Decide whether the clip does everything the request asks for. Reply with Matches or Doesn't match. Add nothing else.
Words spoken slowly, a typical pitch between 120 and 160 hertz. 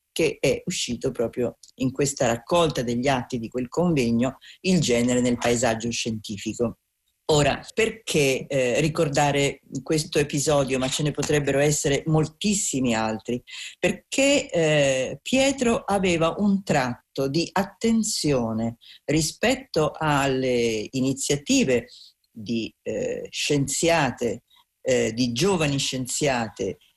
Matches